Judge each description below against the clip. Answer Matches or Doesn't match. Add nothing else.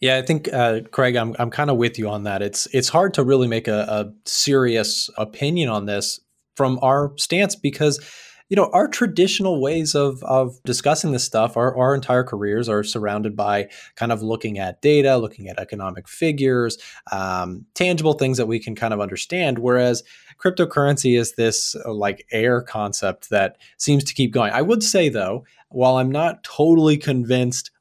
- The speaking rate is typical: Matches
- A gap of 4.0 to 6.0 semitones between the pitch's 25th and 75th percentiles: Matches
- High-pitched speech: Doesn't match